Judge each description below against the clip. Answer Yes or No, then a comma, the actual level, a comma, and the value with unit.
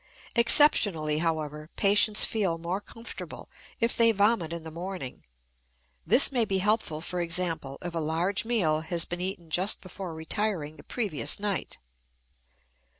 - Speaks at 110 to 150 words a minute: Yes, average, 145 wpm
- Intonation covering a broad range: No, average, 4.5 semitones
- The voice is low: No, medium, 180 Hz